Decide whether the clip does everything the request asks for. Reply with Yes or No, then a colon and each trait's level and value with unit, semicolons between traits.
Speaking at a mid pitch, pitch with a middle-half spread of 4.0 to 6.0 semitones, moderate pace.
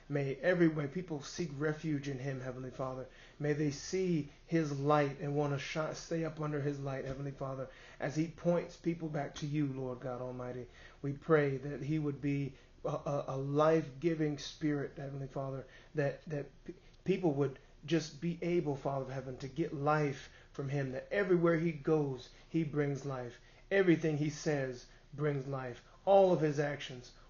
No: medium, 145 Hz; average, 2.8 semitones; average, 175 wpm